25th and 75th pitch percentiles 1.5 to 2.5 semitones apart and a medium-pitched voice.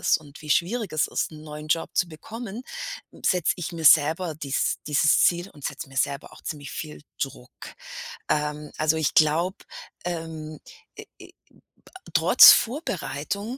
No: average, 2.9 semitones; medium, 155 Hz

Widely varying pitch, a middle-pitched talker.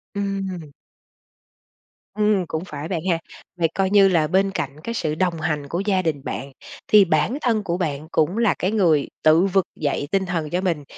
No: average, 3.9 semitones; medium, 175 Hz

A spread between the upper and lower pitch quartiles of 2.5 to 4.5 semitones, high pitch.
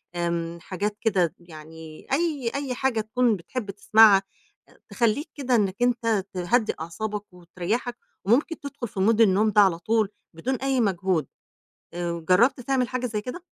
No: wide, 5.5 semitones; high, 215 Hz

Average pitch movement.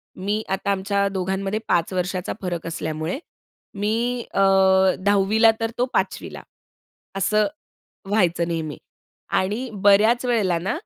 Yes: average, 3.1 semitones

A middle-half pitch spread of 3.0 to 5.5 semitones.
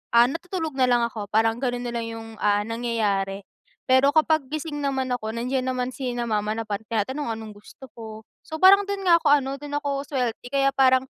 Yes: average, 3.8 semitones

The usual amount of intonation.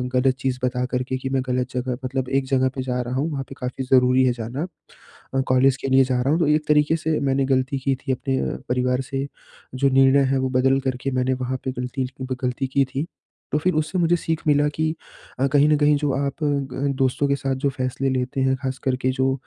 No: narrow, 1.5 semitones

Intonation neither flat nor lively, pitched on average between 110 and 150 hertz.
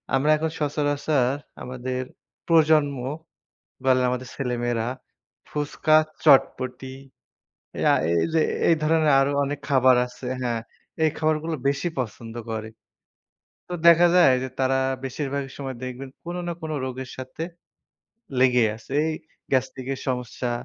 Yes: average, 3.2 semitones; low, 135 Hz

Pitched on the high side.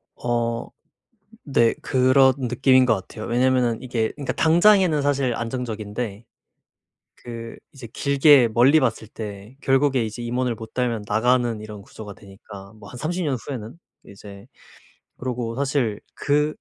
No: low, 120 Hz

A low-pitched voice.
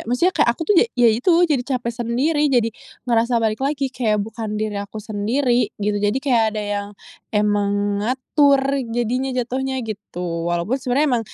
No: high, 235 Hz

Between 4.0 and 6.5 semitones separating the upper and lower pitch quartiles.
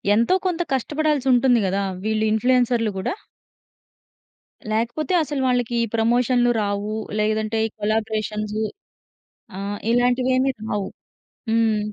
No: average, 2.8 semitones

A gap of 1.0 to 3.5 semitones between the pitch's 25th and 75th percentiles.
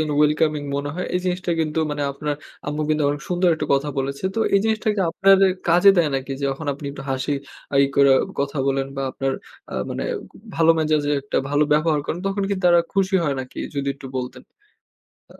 No: average, 3.9 semitones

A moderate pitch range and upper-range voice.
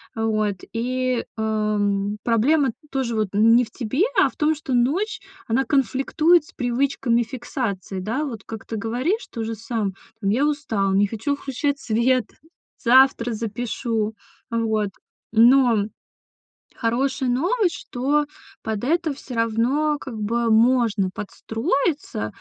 Yes: average, 3.7 semitones; high, 235 Hz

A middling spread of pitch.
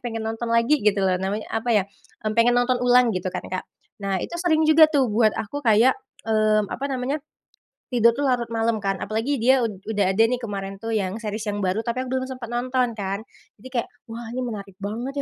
Yes: average, 3.4 semitones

